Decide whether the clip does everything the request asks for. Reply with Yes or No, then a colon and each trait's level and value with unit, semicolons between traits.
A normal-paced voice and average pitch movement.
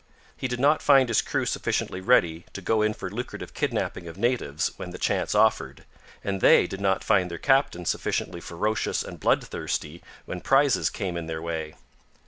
No: average, 180 wpm; wide, 6.3 semitones